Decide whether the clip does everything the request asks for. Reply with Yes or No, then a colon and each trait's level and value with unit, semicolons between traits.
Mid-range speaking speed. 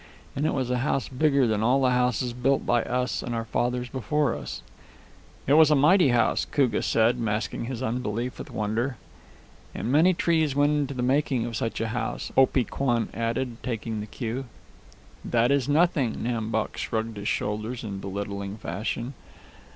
Yes: average, 175 wpm